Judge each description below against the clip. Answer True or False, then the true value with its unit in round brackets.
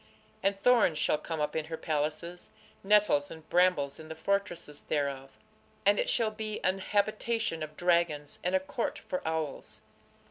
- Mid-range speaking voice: True (170 Hz)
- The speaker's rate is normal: True (165 wpm)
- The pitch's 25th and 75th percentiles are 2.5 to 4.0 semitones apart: False (4.5 semitones)